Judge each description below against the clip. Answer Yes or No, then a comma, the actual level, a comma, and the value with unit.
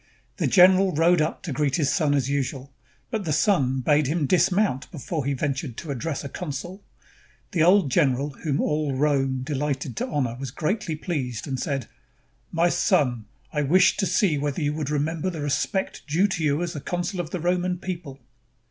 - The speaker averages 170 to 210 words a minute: Yes, average, 185 wpm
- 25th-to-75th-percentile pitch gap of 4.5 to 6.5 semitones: No, average, 4.1 semitones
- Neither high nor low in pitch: Yes, medium, 150 Hz